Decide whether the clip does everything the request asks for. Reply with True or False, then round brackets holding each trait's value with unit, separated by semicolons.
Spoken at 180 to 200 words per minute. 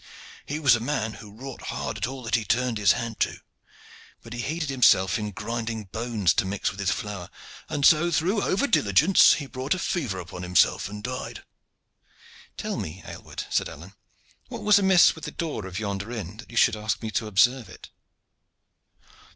True (190 wpm)